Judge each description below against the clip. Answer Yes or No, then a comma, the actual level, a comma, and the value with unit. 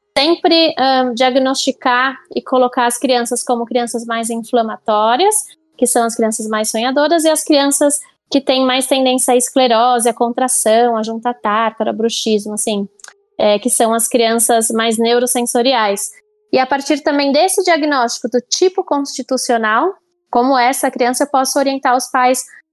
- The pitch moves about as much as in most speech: Yes, average, 3.3 semitones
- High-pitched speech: Yes, very high, 255 Hz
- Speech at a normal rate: Yes, average, 150 wpm